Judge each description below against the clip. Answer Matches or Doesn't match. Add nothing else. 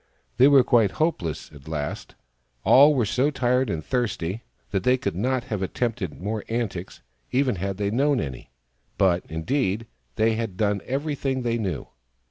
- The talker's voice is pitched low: Matches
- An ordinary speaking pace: Matches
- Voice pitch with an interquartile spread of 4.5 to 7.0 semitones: Matches